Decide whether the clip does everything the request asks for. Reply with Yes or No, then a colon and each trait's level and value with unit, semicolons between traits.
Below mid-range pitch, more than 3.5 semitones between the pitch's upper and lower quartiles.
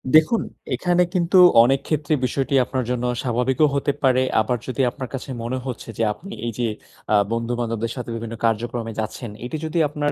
Yes: low, 125 Hz; average, 3.9 semitones